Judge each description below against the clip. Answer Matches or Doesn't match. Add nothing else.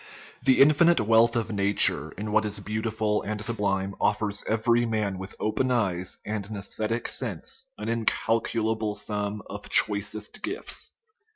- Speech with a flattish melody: Matches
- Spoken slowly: Doesn't match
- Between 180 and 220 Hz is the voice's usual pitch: Doesn't match